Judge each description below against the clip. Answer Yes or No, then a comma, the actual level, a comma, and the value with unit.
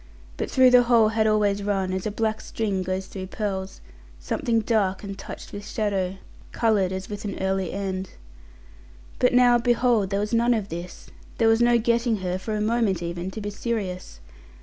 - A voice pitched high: Yes, high, 205 Hz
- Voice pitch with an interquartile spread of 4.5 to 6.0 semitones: No, average, 3.2 semitones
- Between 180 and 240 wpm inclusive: Yes, average, 190 wpm